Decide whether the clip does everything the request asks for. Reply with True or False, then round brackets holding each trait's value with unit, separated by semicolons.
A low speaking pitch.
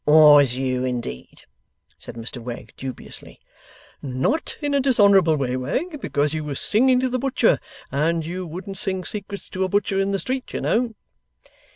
False (175 Hz)